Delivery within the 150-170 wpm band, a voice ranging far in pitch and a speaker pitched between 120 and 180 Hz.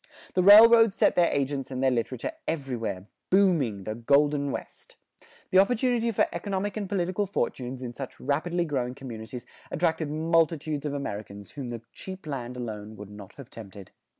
Yes: average, 160 wpm; wide, 7.0 semitones; medium, 140 Hz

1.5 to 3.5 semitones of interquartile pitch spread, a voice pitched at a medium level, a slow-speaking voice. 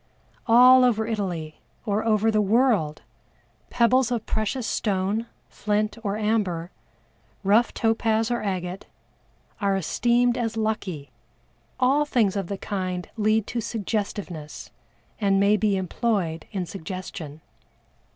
No: average, 3.2 semitones; high, 210 Hz; slow, 120 wpm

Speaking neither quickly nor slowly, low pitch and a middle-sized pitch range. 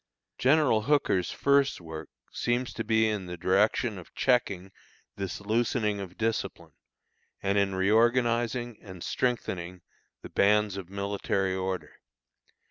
No: slow, 125 wpm; low, 105 Hz; average, 4.0 semitones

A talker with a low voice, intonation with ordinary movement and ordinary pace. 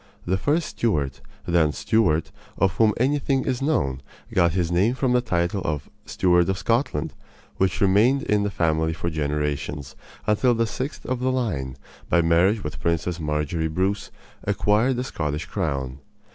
No: very low, 90 Hz; wide, 6.8 semitones; average, 160 wpm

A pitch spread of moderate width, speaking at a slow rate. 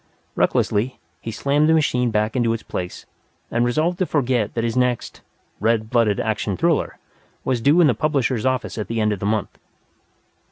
No: average, 4.0 semitones; average, 185 wpm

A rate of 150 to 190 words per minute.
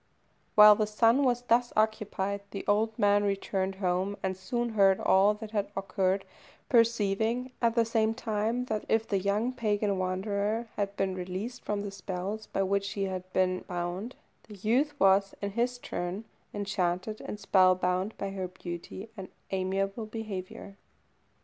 Yes: average, 155 wpm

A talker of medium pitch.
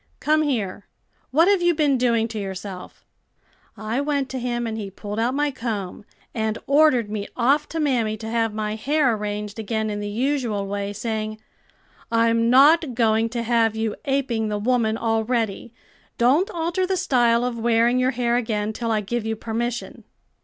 No: high, 230 Hz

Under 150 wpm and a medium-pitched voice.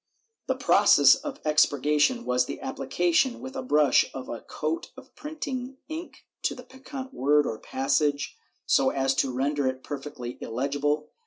No: average, 155 wpm; medium, 150 Hz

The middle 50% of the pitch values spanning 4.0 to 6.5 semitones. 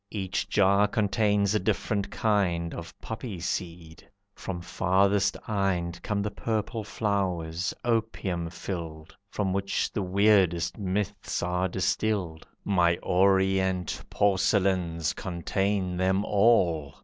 No: average, 2.7 semitones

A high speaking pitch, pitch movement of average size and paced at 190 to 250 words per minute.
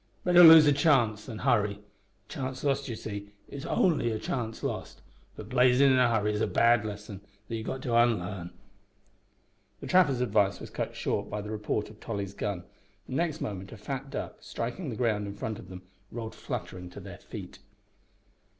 No: low, 115 Hz; average, 4.2 semitones; average, 195 wpm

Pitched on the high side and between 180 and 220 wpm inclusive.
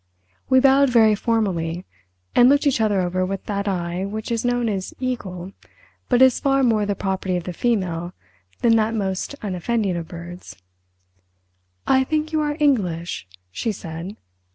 No: high, 205 Hz; average, 160 wpm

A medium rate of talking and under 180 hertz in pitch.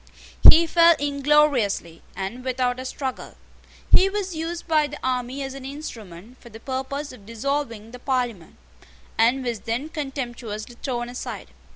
No: average, 150 wpm; very high, 260 Hz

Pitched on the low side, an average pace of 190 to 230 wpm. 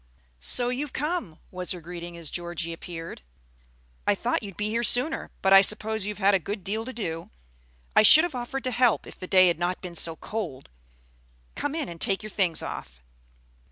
No: high, 195 Hz; average, 200 wpm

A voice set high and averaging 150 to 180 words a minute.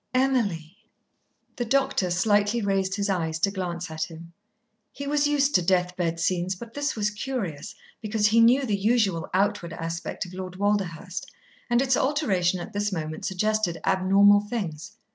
Yes: high, 195 Hz; average, 160 wpm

